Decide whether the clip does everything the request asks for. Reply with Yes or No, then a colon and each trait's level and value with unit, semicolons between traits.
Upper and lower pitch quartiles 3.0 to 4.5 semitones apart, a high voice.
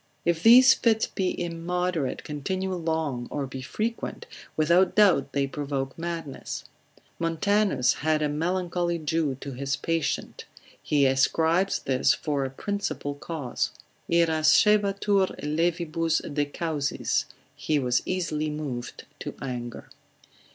No: average, 4.1 semitones; medium, 160 Hz